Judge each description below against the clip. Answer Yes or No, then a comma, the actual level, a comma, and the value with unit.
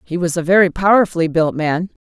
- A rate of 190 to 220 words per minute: Yes, fast, 205 wpm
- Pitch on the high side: No, medium, 175 Hz